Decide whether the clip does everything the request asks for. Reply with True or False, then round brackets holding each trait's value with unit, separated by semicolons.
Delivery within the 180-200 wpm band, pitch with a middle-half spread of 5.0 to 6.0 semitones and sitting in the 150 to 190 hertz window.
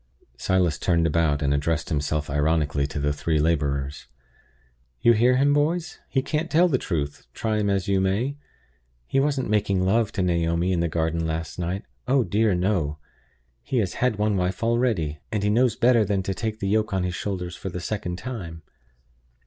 False (190 wpm; 5.3 semitones; 95 Hz)